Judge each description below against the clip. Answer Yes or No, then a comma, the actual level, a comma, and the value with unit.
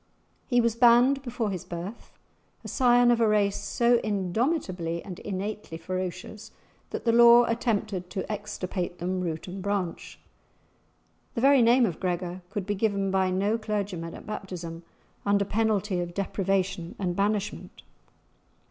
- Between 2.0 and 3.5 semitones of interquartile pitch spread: No, average, 3.9 semitones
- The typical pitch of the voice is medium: No, high, 200 Hz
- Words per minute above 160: No, average, 145 wpm